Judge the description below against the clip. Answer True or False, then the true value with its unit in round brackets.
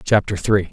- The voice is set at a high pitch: False (100 Hz)